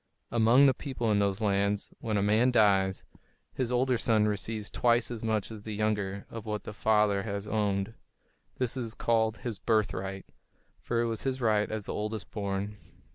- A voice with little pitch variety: Yes, narrow, 2.2 semitones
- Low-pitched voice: Yes, low, 110 Hz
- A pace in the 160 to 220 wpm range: Yes, average, 185 wpm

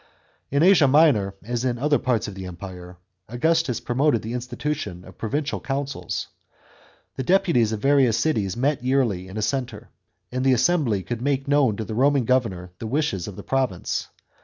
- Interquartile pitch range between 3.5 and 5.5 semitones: Yes, average, 4.9 semitones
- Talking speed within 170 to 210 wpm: Yes, average, 180 wpm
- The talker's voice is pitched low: Yes, low, 125 Hz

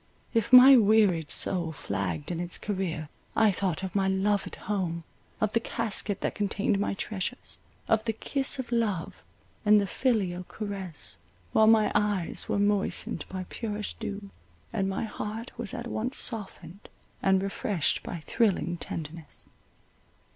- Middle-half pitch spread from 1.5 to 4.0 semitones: Yes, average, 3.3 semitones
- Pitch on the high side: Yes, high, 200 Hz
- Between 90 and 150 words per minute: Yes, average, 145 wpm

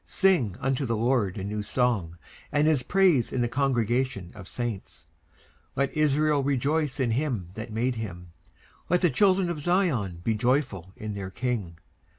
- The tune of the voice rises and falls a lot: Yes, wide, 6.0 semitones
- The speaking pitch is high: No, low, 125 Hz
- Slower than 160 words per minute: No, average, 165 wpm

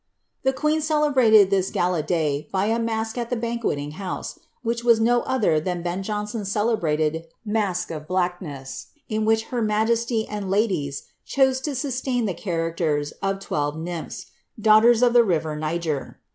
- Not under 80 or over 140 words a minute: No, average, 160 wpm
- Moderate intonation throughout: No, wide, 5.8 semitones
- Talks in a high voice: Yes, high, 210 Hz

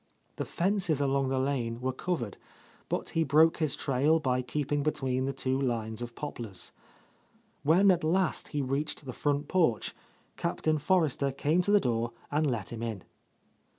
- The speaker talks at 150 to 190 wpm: Yes, average, 170 wpm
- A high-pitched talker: No, medium, 140 Hz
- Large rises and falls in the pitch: No, average, 3.8 semitones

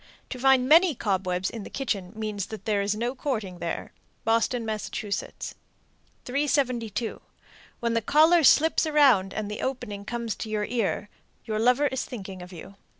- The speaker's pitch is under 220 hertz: No, high, 225 Hz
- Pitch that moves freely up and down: No, average, 4.4 semitones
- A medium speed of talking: Yes, average, 160 wpm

